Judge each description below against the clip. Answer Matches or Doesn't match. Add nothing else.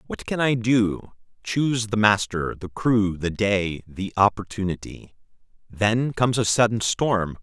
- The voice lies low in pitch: Matches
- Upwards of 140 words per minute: Doesn't match